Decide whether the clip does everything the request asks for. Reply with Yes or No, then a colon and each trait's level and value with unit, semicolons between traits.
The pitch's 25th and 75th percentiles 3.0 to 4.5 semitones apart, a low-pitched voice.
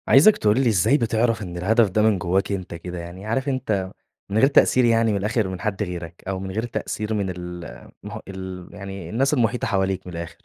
Yes: average, 3.7 semitones; low, 100 Hz